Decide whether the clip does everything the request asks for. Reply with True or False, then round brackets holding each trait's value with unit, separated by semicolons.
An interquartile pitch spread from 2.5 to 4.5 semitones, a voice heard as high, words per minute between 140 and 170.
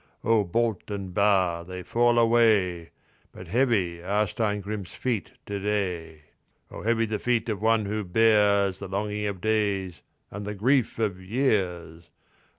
False (3.2 semitones; 105 Hz; 150 wpm)